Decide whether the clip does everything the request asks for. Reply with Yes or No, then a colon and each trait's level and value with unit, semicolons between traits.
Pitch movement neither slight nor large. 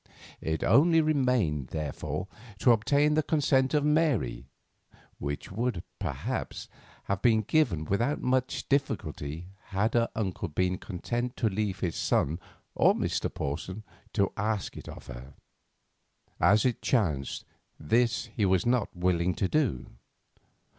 No: wide, 6.8 semitones